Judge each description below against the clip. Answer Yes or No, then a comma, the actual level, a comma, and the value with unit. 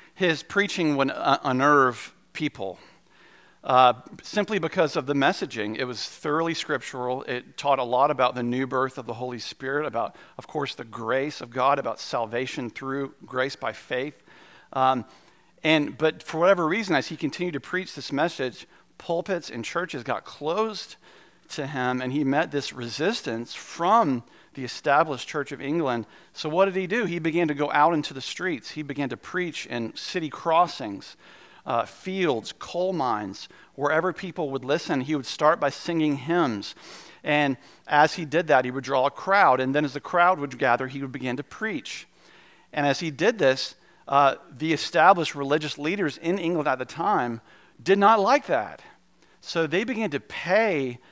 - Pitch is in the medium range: Yes, medium, 145 Hz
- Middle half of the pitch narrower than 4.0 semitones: No, average, 4.6 semitones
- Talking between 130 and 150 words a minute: No, average, 180 wpm